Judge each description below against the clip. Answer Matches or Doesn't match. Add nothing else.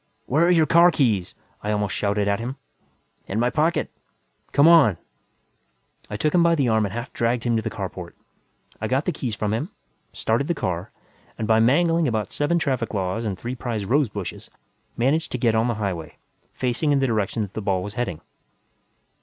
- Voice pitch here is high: Doesn't match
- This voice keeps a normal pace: Matches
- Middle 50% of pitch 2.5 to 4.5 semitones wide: Doesn't match